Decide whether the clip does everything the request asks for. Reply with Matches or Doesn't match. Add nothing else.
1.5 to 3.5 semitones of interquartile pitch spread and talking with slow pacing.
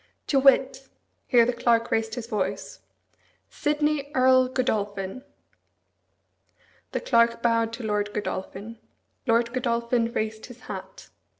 Matches